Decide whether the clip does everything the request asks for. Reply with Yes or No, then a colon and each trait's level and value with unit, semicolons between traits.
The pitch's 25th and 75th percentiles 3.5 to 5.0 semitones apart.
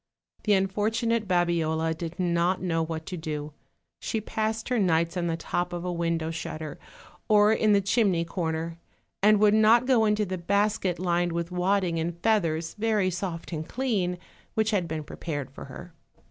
Yes: average, 4.1 semitones